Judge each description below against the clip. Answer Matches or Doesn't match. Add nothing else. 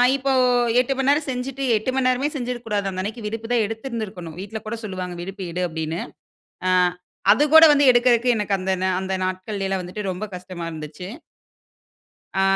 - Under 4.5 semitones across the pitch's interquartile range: Doesn't match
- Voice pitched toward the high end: Matches